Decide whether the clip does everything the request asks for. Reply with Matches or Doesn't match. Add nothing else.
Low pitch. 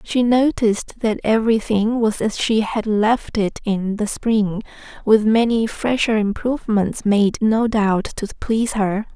Doesn't match